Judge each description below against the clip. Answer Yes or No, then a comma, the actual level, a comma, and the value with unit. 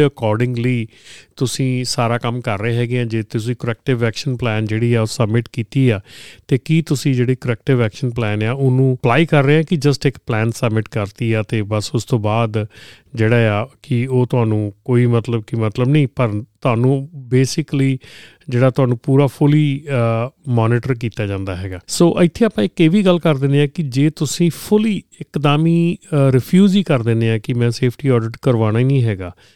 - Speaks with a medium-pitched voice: No, low, 125 Hz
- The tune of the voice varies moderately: Yes, average, 3.6 semitones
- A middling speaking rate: No, fast, 185 wpm